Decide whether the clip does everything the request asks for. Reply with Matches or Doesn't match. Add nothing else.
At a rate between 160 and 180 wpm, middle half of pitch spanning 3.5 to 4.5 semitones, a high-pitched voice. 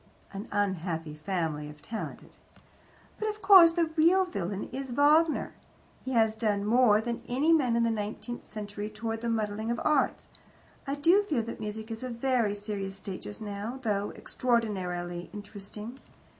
Matches